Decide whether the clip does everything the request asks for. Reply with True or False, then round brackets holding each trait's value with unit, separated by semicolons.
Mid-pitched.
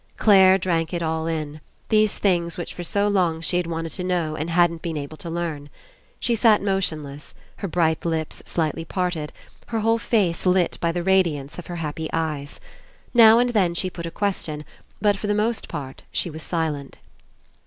True (170 Hz)